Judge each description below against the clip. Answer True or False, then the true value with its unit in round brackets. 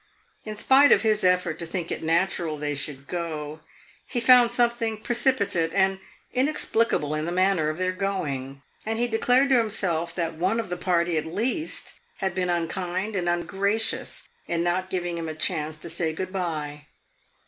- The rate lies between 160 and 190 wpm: True (175 wpm)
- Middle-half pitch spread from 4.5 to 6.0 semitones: True (5.0 semitones)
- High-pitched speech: False (180 Hz)